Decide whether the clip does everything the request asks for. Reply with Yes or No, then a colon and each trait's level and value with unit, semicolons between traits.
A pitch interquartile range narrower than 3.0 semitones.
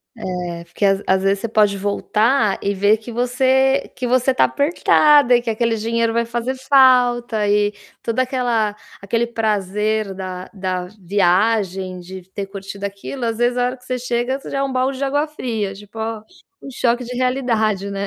No: average, 3.9 semitones